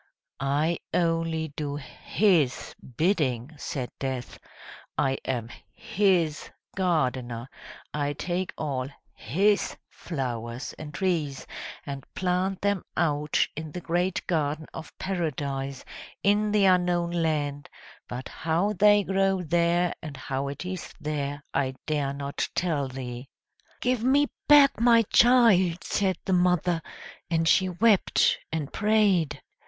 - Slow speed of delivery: Yes, slow, 120 wpm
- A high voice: No, medium, 165 Hz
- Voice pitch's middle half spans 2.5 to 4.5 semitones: No, average, 4.9 semitones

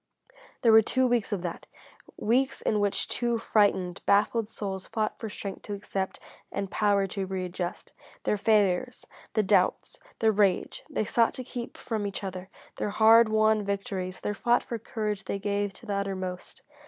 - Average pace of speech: Yes, average, 170 wpm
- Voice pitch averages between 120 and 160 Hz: No, high, 205 Hz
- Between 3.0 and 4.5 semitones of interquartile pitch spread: No, narrow, 2.4 semitones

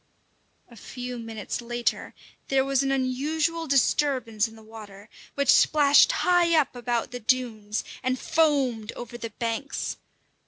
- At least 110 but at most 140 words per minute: Yes, slow, 135 wpm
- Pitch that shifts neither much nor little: Yes, average, 3.7 semitones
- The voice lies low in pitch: No, very high, 250 Hz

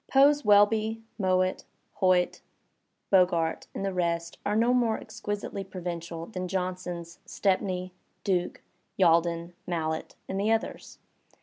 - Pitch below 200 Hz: Yes, medium, 185 Hz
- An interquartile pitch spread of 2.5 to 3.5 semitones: Yes, average, 3.1 semitones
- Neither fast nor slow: No, slow, 120 wpm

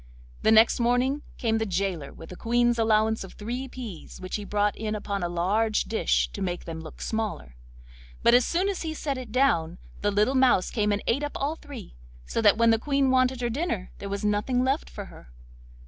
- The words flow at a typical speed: No, fast, 215 wpm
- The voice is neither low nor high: No, high, 220 Hz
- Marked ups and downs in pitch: No, average, 4.2 semitones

